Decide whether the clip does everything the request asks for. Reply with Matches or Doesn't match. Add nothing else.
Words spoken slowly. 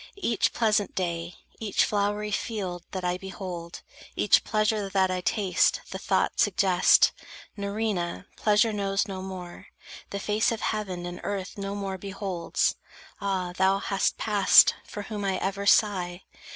Doesn't match